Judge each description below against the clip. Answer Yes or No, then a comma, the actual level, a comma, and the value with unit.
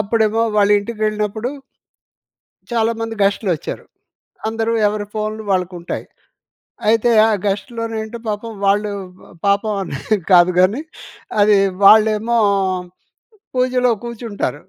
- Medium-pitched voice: No, high, 215 Hz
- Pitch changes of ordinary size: No, narrow, 2.1 semitones